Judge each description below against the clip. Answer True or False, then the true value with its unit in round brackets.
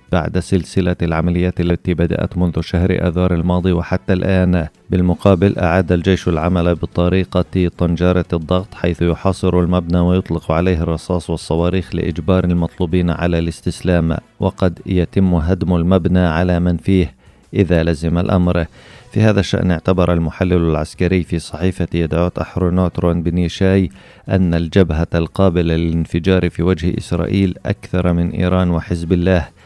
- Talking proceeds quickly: False (125 wpm)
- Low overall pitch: True (90 Hz)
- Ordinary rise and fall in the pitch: False (1.5 semitones)